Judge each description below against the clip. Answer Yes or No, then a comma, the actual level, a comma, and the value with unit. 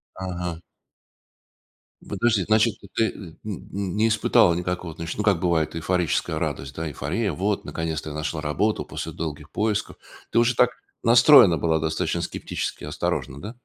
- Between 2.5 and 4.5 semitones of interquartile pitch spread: No, average, 5.0 semitones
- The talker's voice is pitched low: Yes, very low, 90 Hz